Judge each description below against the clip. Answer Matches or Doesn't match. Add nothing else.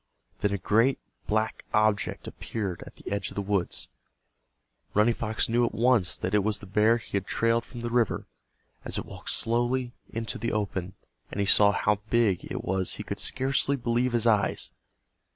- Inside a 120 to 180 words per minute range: Doesn't match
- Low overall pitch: Matches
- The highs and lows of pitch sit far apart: Doesn't match